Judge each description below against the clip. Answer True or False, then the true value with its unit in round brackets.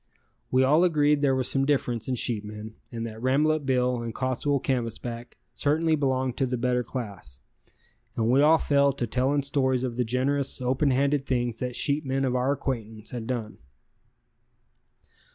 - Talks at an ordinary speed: True (165 wpm)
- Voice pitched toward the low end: True (130 Hz)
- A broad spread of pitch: False (2.8 semitones)